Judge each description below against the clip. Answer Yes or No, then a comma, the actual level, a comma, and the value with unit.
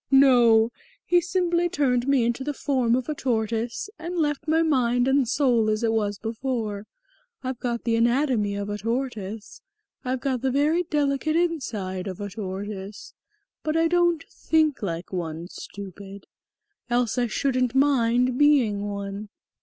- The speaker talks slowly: No, average, 155 wpm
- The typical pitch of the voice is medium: No, high, 245 Hz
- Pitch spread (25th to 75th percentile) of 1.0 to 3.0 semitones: No, average, 5.0 semitones